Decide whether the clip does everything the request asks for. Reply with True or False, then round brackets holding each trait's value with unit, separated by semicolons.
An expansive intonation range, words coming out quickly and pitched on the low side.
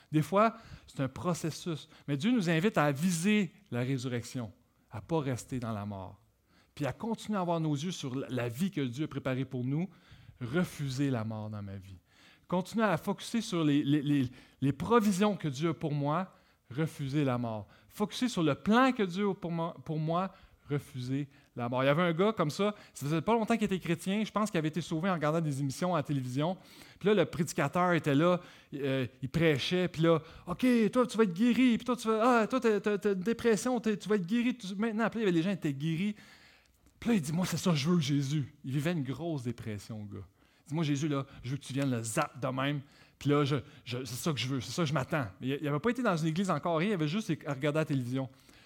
False (5.9 semitones; 240 wpm; 155 Hz)